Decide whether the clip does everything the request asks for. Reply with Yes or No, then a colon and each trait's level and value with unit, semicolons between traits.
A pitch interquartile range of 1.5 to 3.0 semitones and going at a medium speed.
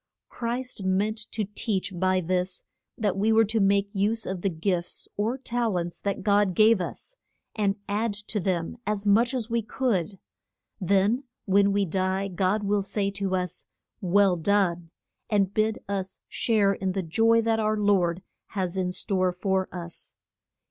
Yes: narrow, 2.5 semitones; average, 165 wpm